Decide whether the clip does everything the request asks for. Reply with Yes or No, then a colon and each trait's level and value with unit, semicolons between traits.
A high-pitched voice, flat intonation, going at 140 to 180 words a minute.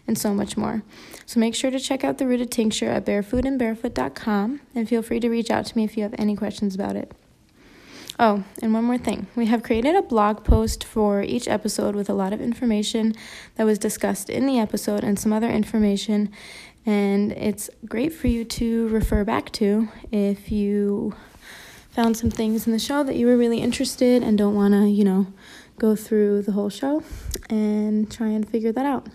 No: high, 220 Hz; narrow, 2.3 semitones; fast, 205 wpm